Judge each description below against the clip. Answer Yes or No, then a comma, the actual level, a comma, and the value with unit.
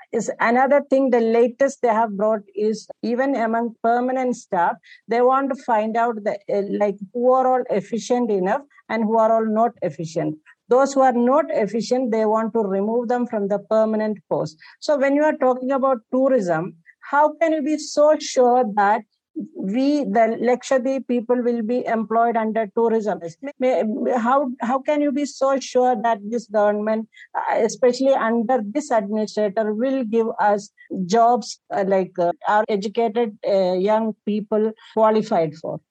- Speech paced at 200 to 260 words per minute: No, average, 155 wpm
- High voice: Yes, high, 230 Hz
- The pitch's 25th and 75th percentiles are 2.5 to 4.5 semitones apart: Yes, average, 3.3 semitones